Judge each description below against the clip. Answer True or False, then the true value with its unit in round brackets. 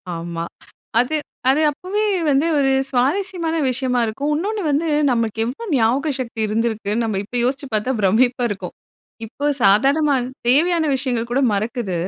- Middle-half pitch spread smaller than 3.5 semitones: False (4.6 semitones)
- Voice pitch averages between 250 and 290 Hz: True (255 Hz)